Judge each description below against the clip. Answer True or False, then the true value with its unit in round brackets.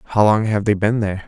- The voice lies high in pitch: False (105 Hz)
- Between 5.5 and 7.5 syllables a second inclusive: True (5.7 syllables/s)